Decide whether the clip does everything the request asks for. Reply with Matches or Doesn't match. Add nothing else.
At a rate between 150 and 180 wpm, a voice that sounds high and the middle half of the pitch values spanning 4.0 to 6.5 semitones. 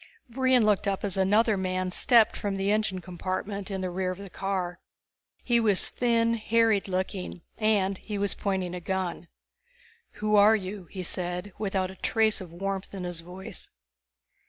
Doesn't match